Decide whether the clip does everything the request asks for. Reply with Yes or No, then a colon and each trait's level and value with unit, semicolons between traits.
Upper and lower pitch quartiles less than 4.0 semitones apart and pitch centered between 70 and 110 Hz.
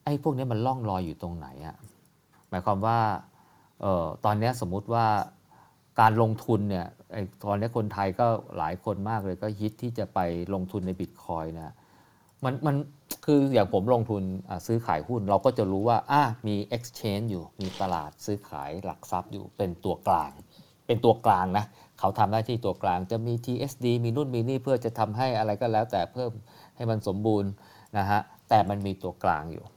Yes: average, 3.5 semitones; low, 105 Hz